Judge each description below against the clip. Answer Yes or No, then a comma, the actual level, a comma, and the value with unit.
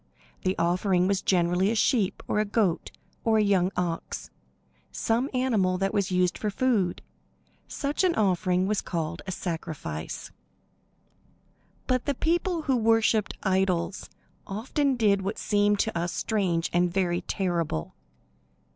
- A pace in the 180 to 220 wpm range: No, average, 140 wpm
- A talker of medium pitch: No, high, 195 Hz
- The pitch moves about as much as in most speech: Yes, average, 3.9 semitones